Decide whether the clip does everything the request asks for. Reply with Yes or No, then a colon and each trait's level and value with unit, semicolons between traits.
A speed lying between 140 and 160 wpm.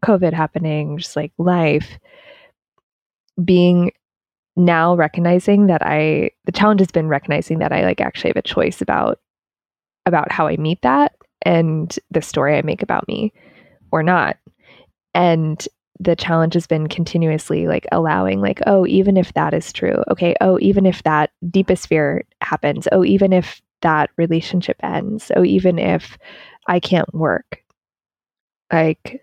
Yes: average, 150 wpm